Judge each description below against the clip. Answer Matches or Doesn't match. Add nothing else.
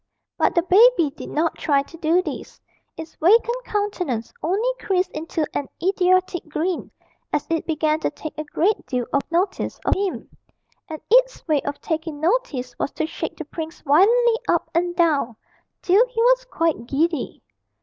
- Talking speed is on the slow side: Doesn't match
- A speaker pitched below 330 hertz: Doesn't match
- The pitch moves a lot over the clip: Doesn't match